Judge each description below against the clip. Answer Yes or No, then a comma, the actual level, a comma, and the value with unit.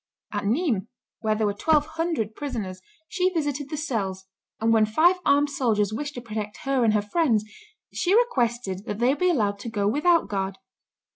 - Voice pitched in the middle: No, high, 235 Hz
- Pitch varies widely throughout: Yes, wide, 6.2 semitones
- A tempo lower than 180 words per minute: No, average, 185 wpm